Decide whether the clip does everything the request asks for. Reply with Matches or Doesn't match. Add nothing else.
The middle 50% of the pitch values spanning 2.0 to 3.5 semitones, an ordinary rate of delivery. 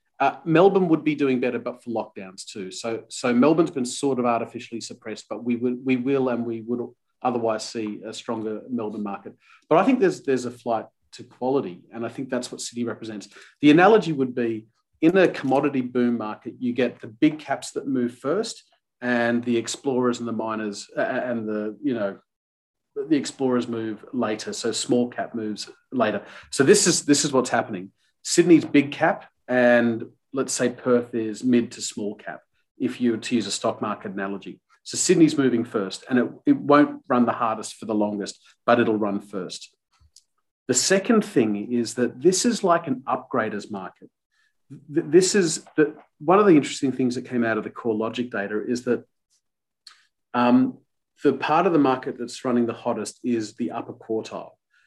Matches